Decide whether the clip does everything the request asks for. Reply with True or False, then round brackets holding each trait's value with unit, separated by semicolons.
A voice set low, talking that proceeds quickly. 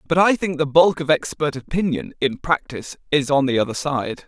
False (150 Hz; 210 wpm)